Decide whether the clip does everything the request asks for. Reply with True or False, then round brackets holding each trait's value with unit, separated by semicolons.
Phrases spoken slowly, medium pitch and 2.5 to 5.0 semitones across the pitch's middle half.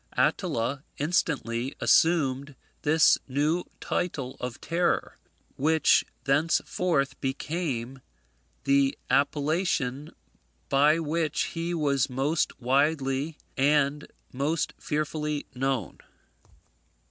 True (80 wpm; 145 Hz; 2.9 semitones)